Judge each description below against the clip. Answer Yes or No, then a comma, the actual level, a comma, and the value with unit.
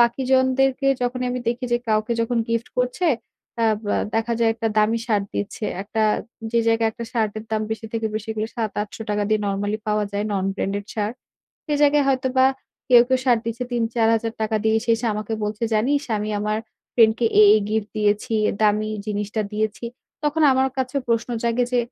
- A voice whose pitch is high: Yes, high, 225 Hz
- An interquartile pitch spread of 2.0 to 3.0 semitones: Yes, narrow, 2.5 semitones